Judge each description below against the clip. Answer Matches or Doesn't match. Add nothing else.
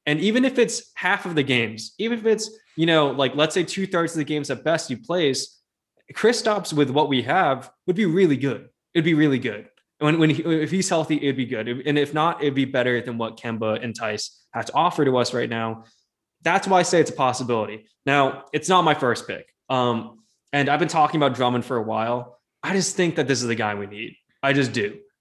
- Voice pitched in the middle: Matches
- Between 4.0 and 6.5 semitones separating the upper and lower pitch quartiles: Matches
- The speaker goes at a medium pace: Doesn't match